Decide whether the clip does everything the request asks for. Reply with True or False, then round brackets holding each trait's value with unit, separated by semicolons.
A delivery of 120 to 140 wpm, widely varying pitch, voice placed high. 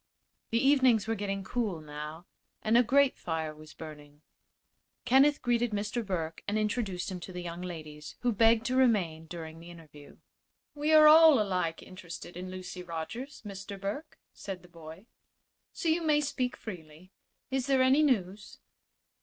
False (160 wpm; 6.8 semitones; 195 Hz)